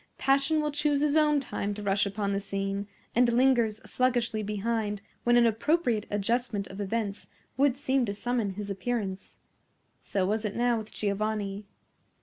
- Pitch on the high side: Yes, high, 220 Hz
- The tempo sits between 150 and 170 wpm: Yes, average, 160 wpm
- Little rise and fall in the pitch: No, average, 3.7 semitones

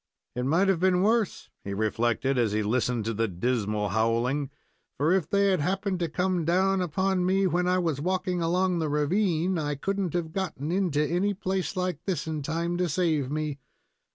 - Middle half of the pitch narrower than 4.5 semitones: No, average, 5.1 semitones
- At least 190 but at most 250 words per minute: Yes, average, 195 wpm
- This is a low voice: No, medium, 170 Hz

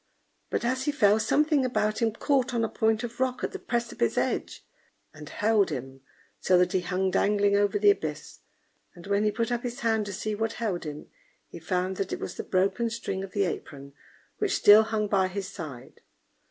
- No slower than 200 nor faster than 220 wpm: Yes, fast, 205 wpm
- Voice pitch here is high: Yes, high, 205 Hz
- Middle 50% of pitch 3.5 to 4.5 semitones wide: Yes, average, 3.9 semitones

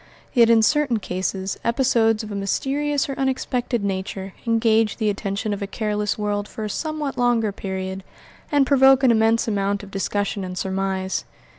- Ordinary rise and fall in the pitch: Yes, average, 3.6 semitones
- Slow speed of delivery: No, average, 165 wpm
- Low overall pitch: No, high, 215 Hz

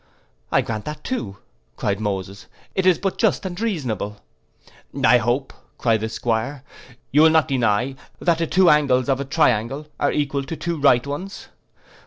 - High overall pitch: No, low, 135 Hz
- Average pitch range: No, wide, 6.1 semitones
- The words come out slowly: No, average, 165 wpm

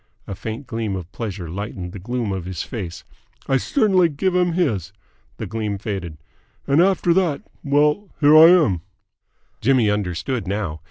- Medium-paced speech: Yes, average, 160 wpm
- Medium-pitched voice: No, low, 115 Hz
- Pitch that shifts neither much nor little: No, wide, 7.7 semitones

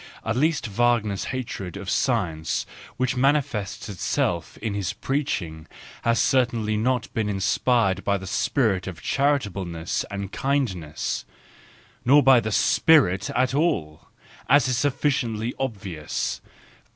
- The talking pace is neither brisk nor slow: No, slow, 120 wpm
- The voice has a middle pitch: No, low, 110 Hz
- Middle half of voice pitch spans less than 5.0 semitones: No, average, 5.3 semitones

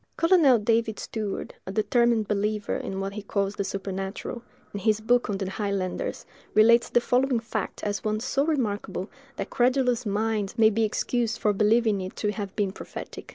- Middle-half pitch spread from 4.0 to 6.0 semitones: No, average, 2.9 semitones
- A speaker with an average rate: Yes, average, 175 wpm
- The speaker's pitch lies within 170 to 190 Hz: No, high, 215 Hz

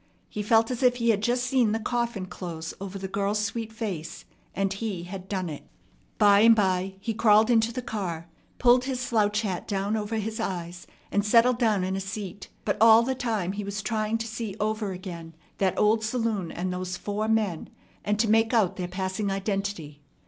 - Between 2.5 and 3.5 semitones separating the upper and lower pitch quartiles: Yes, average, 2.9 semitones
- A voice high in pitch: Yes, high, 210 Hz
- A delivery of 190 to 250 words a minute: Yes, average, 200 wpm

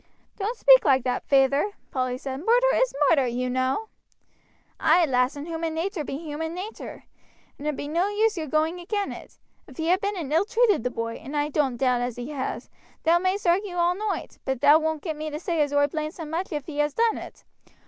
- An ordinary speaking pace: No, fast, 225 wpm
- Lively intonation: No, average, 4.8 semitones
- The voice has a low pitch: No, very high, 310 Hz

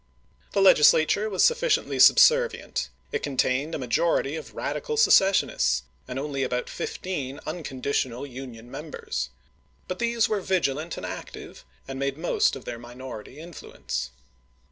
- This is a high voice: No, medium, 145 Hz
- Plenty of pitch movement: Yes, wide, 6.6 semitones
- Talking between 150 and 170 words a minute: No, average, 140 wpm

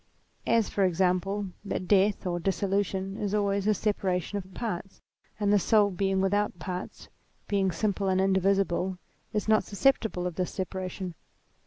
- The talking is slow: No, average, 150 wpm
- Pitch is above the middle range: Yes, high, 195 Hz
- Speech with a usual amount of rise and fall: No, narrow, 1.7 semitones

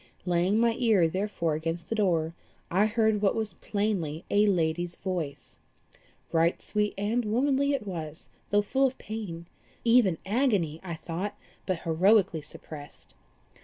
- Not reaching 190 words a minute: Yes, average, 140 wpm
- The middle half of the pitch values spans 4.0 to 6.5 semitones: Yes, average, 4.6 semitones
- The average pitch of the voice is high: Yes, high, 195 Hz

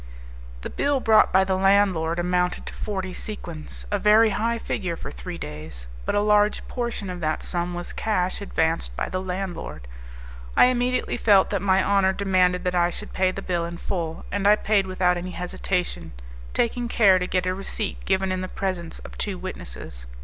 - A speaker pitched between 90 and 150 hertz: No, medium, 185 Hz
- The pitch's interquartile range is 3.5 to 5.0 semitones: No, narrow, 2.6 semitones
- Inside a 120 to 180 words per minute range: No, average, 190 wpm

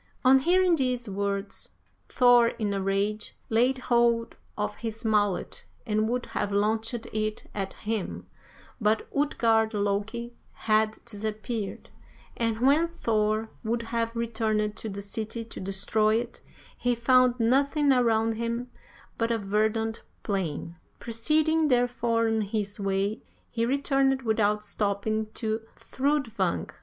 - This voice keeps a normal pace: No, slow, 125 wpm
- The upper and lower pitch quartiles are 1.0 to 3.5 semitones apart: Yes, narrow, 2.4 semitones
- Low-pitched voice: No, high, 225 Hz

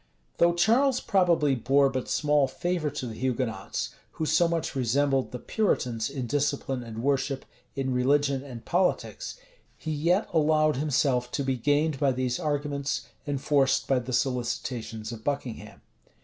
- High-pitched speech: No, medium, 140 Hz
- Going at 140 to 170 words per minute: Yes, average, 150 wpm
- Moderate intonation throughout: Yes, average, 3.3 semitones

